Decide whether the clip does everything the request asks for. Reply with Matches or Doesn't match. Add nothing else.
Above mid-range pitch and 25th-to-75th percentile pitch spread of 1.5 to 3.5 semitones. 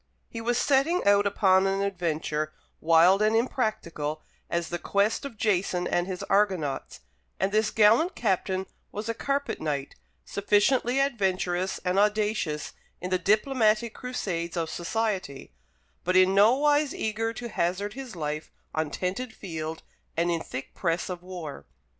Doesn't match